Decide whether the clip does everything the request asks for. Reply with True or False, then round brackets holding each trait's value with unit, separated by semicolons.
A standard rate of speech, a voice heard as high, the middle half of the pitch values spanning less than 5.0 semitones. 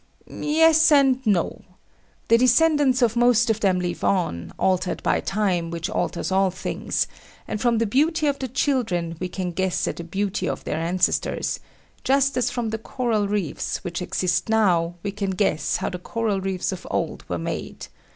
False (180 wpm; 205 Hz; 5.5 semitones)